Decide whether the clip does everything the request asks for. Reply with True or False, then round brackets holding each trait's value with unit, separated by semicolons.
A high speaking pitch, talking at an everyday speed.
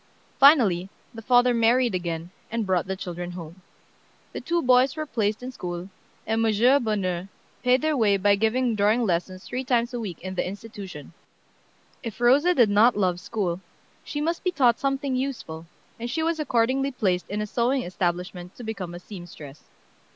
True (220 Hz; 175 wpm)